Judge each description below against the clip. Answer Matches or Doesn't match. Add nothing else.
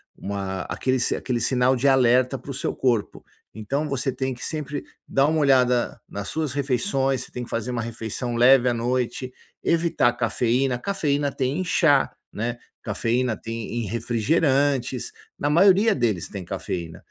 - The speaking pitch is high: Doesn't match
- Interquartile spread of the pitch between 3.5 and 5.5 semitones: Doesn't match